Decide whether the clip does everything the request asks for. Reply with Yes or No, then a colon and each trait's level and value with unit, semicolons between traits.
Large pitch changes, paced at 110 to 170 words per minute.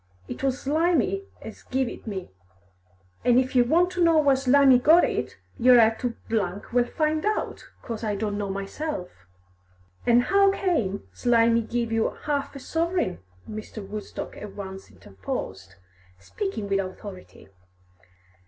Yes: wide, 6.9 semitones; average, 155 wpm